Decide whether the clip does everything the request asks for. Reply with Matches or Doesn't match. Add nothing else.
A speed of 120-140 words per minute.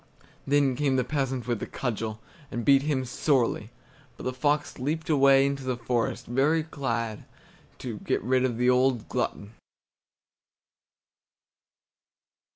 Matches